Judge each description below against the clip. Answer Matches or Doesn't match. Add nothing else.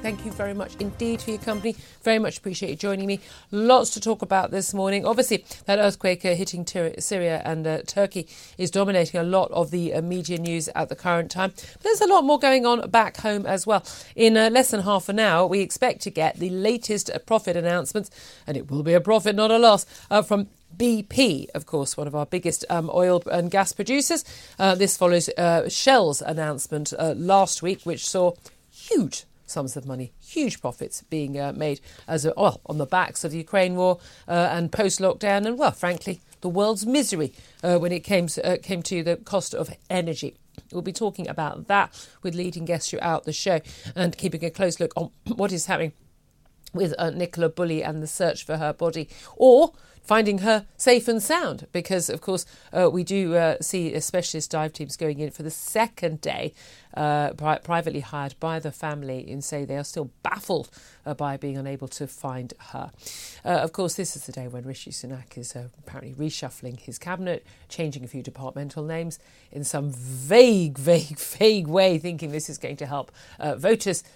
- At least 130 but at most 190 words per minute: Doesn't match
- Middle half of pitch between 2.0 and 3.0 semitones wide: Doesn't match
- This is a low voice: Doesn't match